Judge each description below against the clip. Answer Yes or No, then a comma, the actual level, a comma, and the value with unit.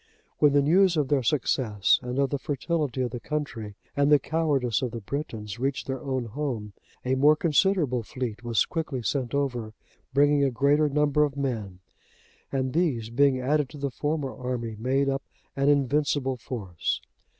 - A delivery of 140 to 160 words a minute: No, average, 170 wpm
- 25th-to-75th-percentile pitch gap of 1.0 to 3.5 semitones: Yes, average, 3.2 semitones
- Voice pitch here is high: No, low, 135 Hz